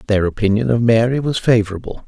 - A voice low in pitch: Yes, low, 115 Hz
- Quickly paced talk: No, average, 175 wpm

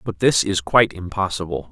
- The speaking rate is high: No, average, 175 wpm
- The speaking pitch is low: Yes, very low, 95 Hz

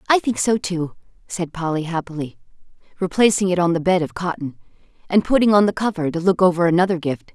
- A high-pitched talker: No, medium, 175 Hz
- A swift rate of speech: No, average, 195 wpm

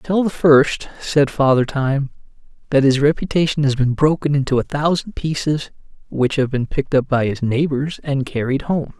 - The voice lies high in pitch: No, medium, 140 Hz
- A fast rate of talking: No, average, 180 wpm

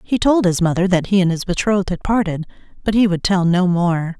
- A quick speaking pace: Yes, fast, 245 wpm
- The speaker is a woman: Yes, female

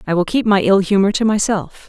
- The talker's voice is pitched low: No, high, 195 Hz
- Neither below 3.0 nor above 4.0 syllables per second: No, 5.8 syllables/s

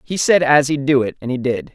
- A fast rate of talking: Yes, fast, 310 wpm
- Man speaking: Yes, male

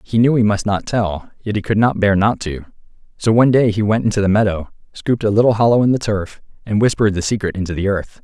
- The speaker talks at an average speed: No, fast, 255 wpm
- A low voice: Yes, low, 105 Hz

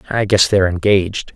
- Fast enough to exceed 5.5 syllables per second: Yes, 6.1 syllables/s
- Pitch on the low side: Yes, very low, 95 Hz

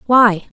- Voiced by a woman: Yes, female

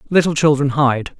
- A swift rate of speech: No, average, 150 wpm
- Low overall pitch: No, medium, 145 Hz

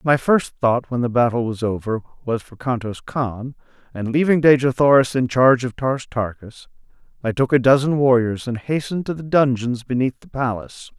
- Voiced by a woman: No, male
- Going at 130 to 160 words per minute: No, average, 185 wpm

